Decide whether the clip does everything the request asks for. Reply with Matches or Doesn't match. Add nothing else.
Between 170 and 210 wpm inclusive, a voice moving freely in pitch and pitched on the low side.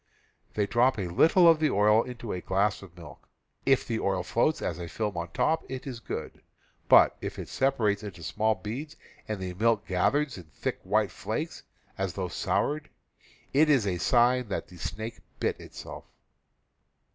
Matches